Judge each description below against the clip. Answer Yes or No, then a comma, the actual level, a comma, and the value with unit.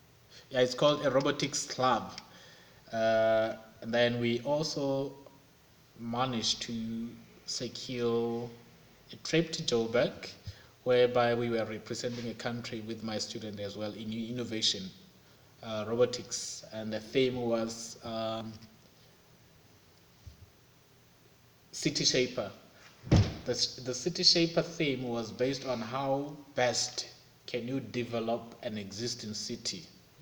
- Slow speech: Yes, slow, 110 wpm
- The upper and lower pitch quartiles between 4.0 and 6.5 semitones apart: No, narrow, 2.4 semitones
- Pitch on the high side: No, low, 120 Hz